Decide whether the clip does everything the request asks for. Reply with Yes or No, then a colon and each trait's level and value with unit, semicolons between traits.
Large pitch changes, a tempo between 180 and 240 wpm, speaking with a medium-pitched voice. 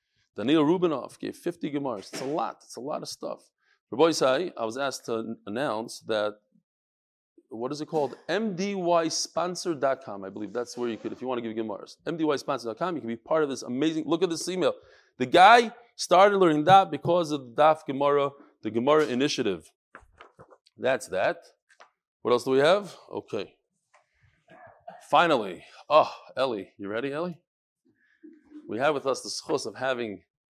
No: wide, 6.3 semitones; average, 165 wpm; medium, 150 Hz